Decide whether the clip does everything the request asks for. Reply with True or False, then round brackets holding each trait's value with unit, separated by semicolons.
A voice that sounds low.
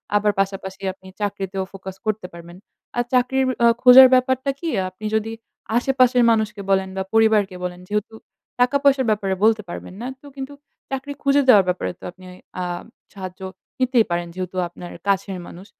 False (210 Hz)